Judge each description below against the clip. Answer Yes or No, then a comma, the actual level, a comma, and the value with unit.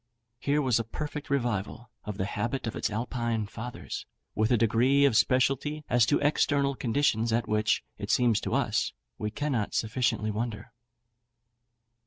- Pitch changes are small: No, average, 3.9 semitones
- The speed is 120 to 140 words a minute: No, average, 155 wpm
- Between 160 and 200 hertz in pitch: No, low, 120 Hz